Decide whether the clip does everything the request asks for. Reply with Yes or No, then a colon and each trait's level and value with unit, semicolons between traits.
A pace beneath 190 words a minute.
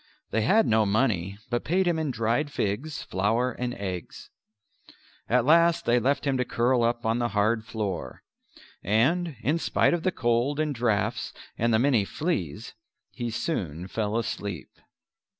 Yes: average, 160 wpm